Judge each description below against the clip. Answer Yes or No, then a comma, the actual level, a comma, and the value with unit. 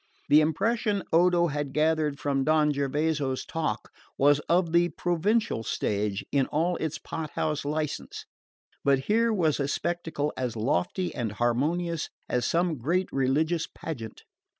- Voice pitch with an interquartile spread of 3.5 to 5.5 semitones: Yes, average, 3.9 semitones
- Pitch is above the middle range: No, medium, 155 Hz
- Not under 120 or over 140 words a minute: Yes, slow, 135 wpm